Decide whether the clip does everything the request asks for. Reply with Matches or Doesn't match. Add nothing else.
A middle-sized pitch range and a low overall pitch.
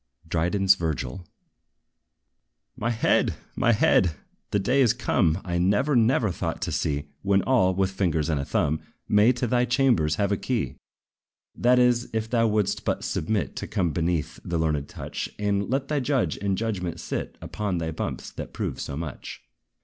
Doesn't match